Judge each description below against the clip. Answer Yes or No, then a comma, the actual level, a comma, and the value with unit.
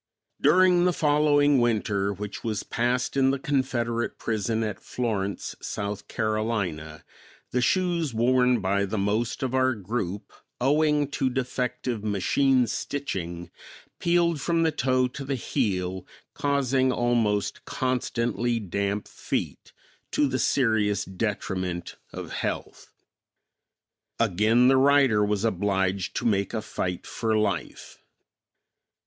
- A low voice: Yes, low, 115 Hz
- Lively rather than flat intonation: No, average, 4.7 semitones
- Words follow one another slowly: Yes, slow, 120 wpm